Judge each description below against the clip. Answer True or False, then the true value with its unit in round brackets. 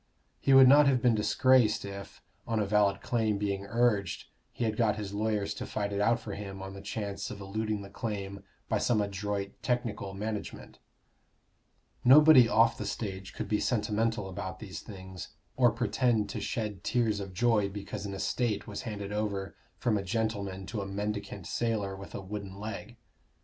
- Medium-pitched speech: False (105 Hz)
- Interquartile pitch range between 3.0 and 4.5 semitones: False (2.4 semitones)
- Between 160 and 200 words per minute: True (180 wpm)